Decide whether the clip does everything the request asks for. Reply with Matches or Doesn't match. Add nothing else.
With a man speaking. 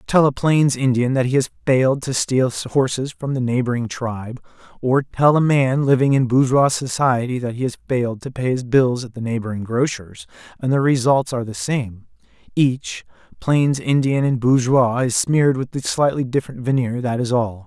Matches